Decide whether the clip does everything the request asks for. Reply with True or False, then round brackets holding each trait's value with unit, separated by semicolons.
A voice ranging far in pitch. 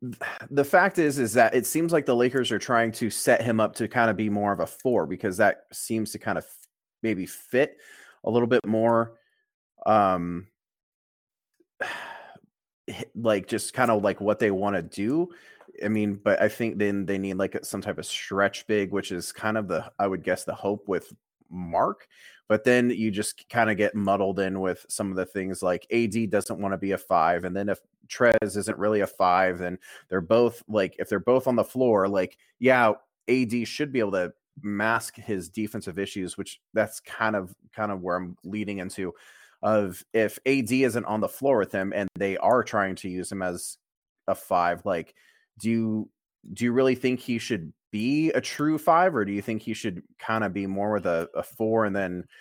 False (3.2 semitones)